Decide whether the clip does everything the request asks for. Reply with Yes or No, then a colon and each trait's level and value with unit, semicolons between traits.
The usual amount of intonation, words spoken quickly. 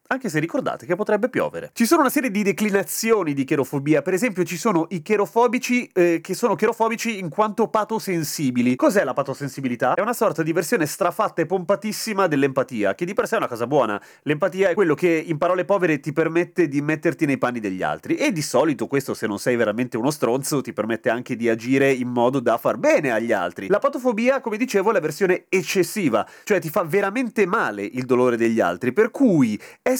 No: wide, 7.6 semitones; fast, 210 wpm